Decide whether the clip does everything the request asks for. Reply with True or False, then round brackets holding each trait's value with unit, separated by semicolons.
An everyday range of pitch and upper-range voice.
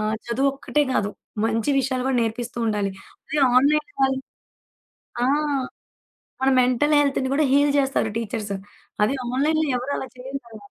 True (3.5 semitones; 260 Hz)